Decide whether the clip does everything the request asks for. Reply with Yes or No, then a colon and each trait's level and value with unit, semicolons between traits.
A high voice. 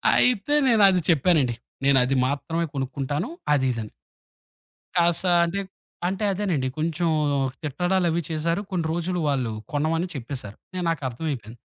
No: medium, 160 Hz